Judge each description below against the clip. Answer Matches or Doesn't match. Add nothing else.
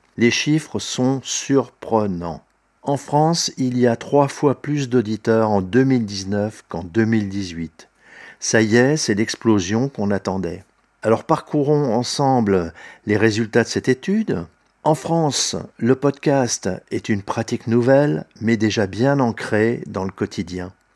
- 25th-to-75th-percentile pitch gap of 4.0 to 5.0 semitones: Matches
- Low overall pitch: Matches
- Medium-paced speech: Doesn't match